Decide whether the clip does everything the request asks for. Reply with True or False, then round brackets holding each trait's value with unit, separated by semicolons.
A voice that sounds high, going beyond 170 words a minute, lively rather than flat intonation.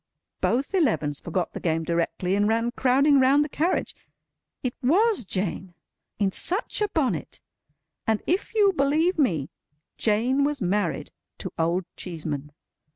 False (235 Hz; 140 wpm; 8.7 semitones)